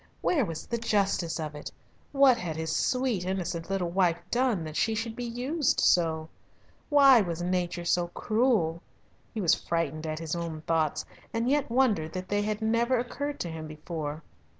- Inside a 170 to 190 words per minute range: Yes, average, 175 wpm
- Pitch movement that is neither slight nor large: No, wide, 6.3 semitones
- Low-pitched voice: No, medium, 185 Hz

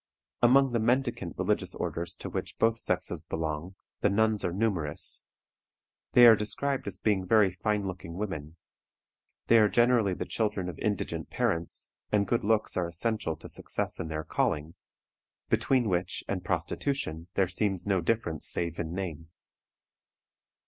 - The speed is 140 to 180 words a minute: Yes, average, 150 wpm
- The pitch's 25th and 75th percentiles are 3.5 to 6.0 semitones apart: Yes, average, 4.9 semitones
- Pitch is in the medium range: No, low, 100 Hz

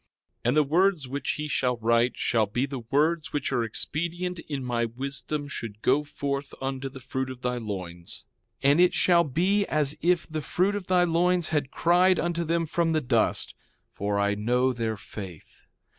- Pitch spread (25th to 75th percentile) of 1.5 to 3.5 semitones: No, wide, 5.6 semitones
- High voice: No, medium, 140 Hz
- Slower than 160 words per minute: No, average, 190 wpm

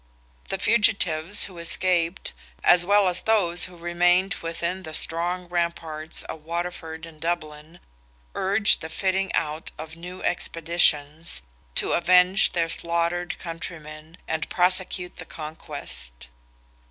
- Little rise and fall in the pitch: Yes, narrow, 2.0 semitones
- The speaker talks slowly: Yes, slow, 120 wpm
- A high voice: No, medium, 170 Hz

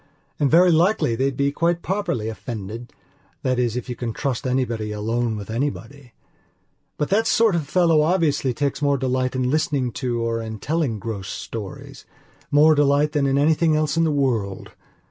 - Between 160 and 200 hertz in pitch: No, low, 135 Hz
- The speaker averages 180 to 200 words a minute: No, average, 165 wpm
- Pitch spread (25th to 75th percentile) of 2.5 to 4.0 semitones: No, average, 4.8 semitones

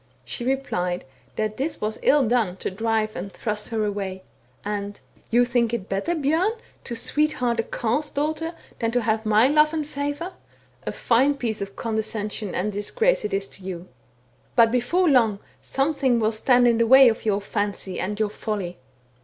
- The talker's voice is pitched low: No, high, 230 Hz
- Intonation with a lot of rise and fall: No, average, 4.6 semitones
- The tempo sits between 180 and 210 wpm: Yes, average, 185 wpm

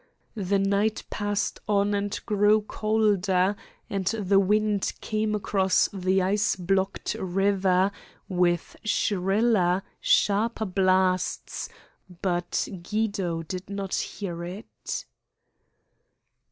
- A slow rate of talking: Yes, slow, 95 wpm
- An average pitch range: No, narrow, 2.0 semitones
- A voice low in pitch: No, high, 195 Hz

